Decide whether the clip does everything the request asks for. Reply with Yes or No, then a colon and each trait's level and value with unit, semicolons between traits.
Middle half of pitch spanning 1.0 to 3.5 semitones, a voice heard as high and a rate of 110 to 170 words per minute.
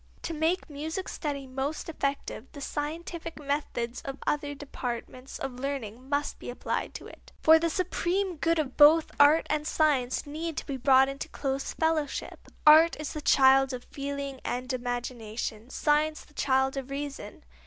Yes: average, 2.7 semitones; very high, 285 Hz; average, 165 wpm